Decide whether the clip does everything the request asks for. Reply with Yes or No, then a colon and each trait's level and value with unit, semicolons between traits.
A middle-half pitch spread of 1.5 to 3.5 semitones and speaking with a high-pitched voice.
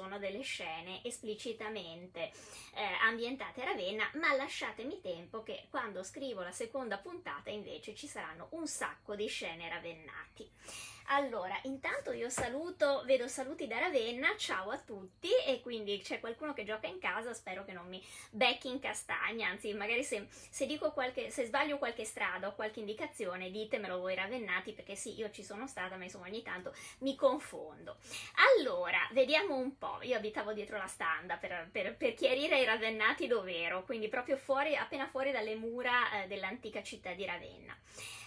No: wide, 5.5 semitones; high, 225 Hz